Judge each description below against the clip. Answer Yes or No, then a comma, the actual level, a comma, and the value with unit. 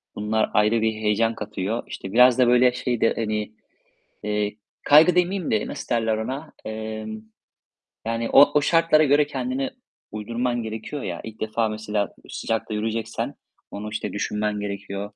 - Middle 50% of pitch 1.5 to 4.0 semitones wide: Yes, average, 2.8 semitones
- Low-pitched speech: Yes, low, 110 Hz